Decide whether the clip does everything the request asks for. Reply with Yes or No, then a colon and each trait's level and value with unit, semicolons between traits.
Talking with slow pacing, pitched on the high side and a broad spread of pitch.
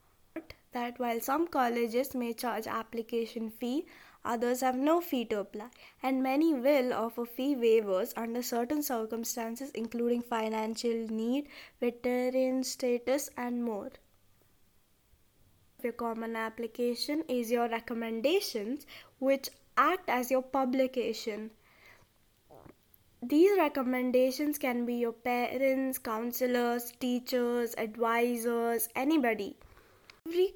No: slow, 100 wpm; high, 240 Hz; narrow, 2.4 semitones